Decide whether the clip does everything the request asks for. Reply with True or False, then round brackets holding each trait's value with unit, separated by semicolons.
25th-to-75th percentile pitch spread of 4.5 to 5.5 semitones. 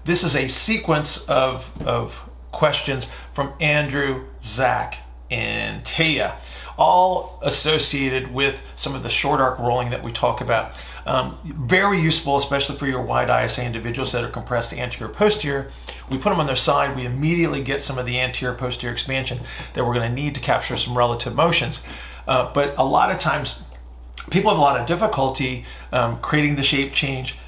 False (3.0 semitones)